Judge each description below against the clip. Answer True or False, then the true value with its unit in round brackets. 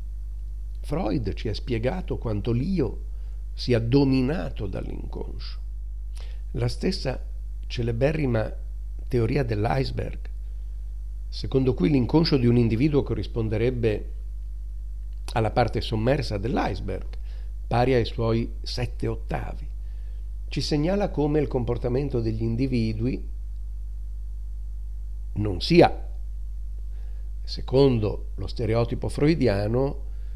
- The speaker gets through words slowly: True (85 wpm)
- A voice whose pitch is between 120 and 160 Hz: False (105 Hz)